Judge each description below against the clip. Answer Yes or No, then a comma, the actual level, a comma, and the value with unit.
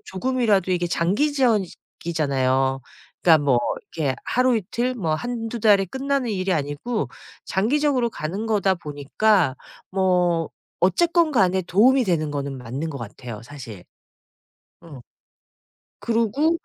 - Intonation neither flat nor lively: No, wide, 8.1 semitones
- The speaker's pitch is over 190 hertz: No, medium, 185 Hz